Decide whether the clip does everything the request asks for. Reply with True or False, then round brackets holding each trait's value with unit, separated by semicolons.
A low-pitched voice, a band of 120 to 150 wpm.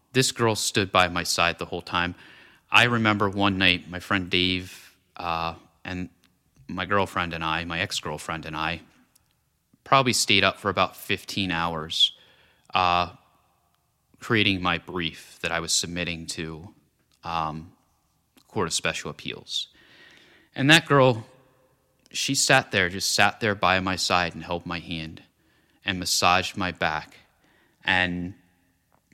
True (90 Hz; 140 wpm)